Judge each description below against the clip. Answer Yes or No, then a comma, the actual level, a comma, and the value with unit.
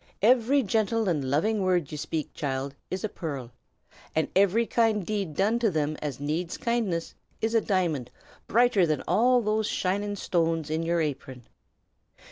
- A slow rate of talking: No, average, 160 wpm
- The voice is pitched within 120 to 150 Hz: No, medium, 185 Hz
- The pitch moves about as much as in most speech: No, wide, 5.9 semitones